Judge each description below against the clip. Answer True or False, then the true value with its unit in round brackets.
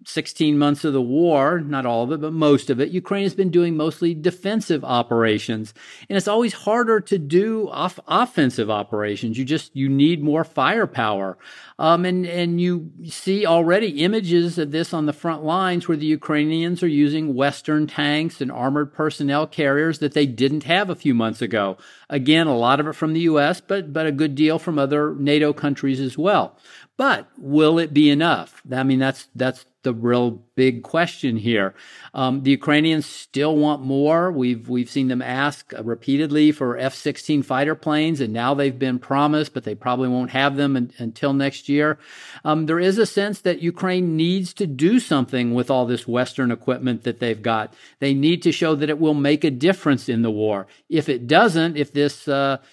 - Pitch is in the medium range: True (145 Hz)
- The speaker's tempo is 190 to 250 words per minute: True (195 wpm)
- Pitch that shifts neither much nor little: True (3.9 semitones)